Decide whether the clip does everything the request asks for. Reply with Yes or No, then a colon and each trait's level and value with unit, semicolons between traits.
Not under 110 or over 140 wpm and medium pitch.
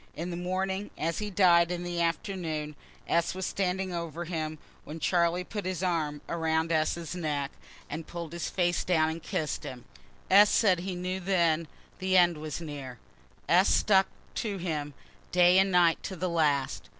No: average, 175 wpm; medium, 170 Hz